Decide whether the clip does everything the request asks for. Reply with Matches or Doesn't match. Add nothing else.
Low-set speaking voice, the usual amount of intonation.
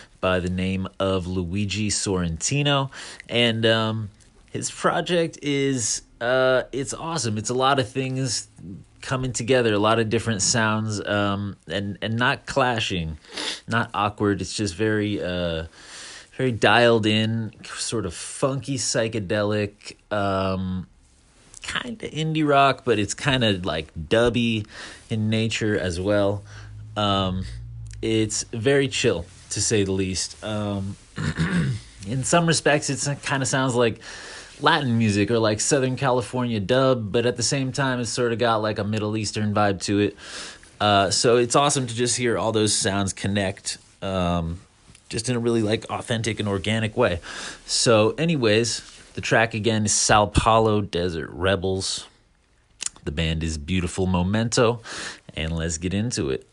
Matches